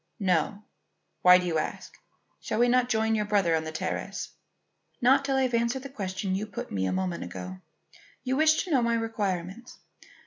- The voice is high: Yes, high, 215 Hz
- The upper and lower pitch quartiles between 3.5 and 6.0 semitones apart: Yes, average, 5.2 semitones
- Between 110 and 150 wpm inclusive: No, average, 195 wpm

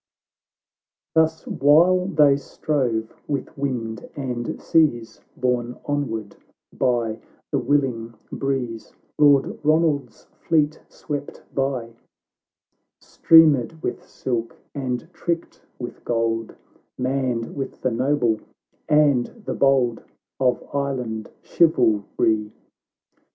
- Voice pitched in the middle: No, low, 130 Hz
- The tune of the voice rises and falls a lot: No, average, 3.8 semitones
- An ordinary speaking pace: No, slow, 95 wpm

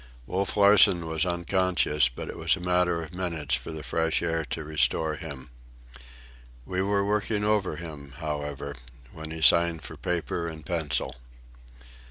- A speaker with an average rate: Yes, average, 155 wpm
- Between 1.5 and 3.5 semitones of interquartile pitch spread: Yes, average, 2.8 semitones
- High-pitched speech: No, very low, 80 Hz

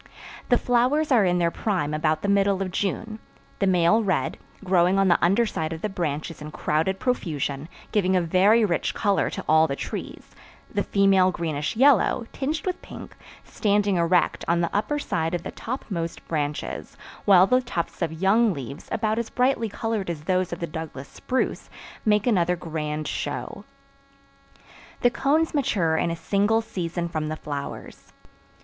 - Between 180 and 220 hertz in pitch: Yes, medium, 185 Hz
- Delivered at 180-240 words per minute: No, average, 170 wpm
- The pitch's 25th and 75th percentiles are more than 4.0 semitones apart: Yes, average, 5.0 semitones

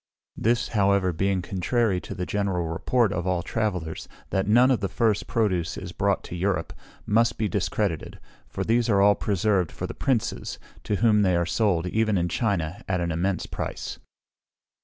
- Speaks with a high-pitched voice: No, low, 100 Hz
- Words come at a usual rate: Yes, average, 180 wpm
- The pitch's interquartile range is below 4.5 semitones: Yes, average, 3.5 semitones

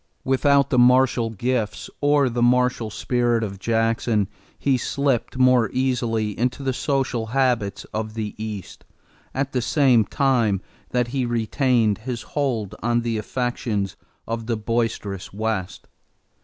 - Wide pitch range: No, average, 2.8 semitones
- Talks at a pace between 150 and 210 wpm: No, slow, 135 wpm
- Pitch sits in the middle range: No, low, 120 Hz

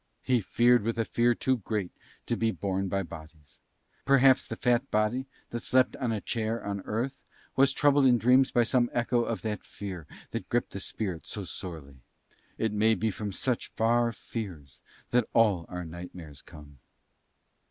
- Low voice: Yes, low, 110 Hz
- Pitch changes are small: No, average, 4.5 semitones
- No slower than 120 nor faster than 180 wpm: Yes, average, 175 wpm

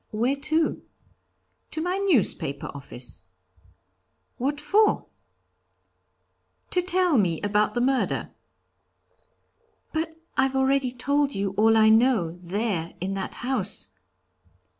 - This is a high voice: Yes, very high, 250 Hz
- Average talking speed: No, slow, 100 wpm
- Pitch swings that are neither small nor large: No, wide, 6.5 semitones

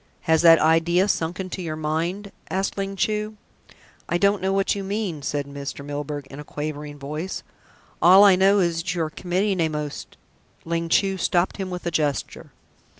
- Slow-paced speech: No, average, 190 wpm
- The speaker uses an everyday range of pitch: Yes, average, 4.0 semitones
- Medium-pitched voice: Yes, medium, 170 Hz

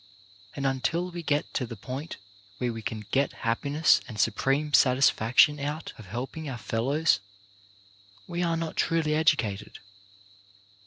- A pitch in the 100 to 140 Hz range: Yes, low, 135 Hz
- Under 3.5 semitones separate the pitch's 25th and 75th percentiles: No, average, 5.1 semitones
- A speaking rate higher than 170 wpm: No, average, 145 wpm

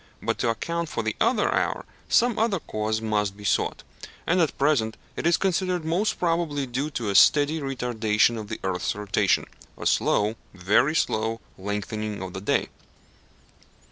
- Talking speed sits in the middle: Yes, average, 165 wpm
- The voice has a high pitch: No, low, 115 Hz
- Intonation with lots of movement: Yes, wide, 7.4 semitones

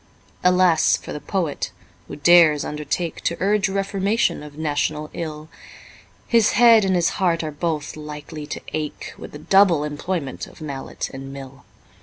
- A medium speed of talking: Yes, average, 155 wpm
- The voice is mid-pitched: Yes, medium, 155 Hz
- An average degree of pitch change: Yes, average, 3.9 semitones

